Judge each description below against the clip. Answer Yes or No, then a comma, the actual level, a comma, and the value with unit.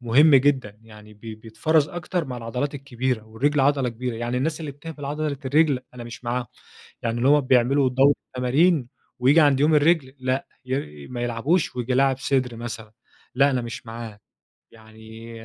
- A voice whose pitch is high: No, low, 130 Hz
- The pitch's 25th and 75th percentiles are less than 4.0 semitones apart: Yes, average, 3.6 semitones